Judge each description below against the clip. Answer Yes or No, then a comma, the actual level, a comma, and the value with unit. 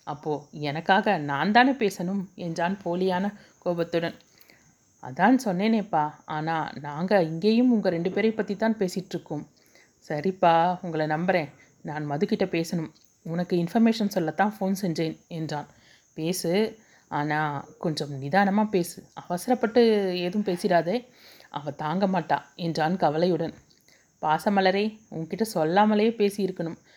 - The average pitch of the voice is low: No, medium, 180 Hz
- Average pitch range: Yes, average, 4.2 semitones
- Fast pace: No, average, 105 wpm